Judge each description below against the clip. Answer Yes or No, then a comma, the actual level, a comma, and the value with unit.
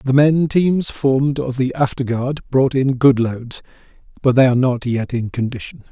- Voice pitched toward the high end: No, low, 130 Hz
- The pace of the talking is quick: No, average, 195 wpm